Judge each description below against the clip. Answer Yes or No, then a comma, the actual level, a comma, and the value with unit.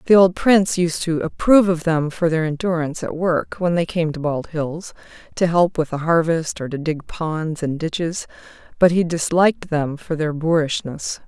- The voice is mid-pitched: Yes, medium, 165 Hz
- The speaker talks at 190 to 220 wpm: Yes, average, 195 wpm